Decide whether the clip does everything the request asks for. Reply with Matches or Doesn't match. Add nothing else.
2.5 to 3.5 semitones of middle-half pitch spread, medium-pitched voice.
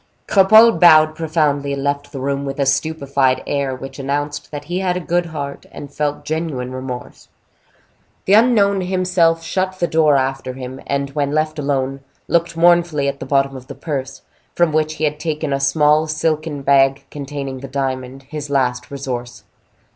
Matches